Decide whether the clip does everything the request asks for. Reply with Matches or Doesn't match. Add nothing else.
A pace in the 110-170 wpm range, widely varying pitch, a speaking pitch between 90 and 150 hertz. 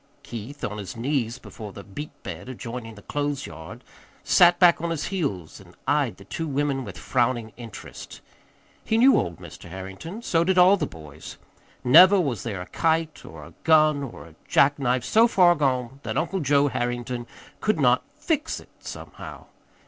Doesn't match